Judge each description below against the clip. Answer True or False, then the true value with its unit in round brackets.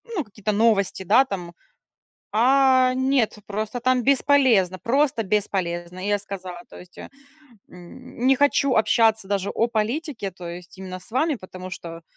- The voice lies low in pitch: False (215 Hz)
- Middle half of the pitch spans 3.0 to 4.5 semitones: False (5.5 semitones)